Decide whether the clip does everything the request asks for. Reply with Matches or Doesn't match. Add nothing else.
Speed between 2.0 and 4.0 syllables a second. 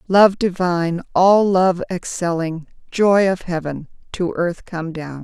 Matches